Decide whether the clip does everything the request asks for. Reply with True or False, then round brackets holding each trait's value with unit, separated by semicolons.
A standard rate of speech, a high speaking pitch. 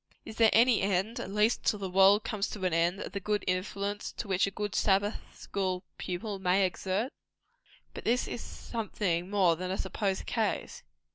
True (190 wpm; 195 Hz)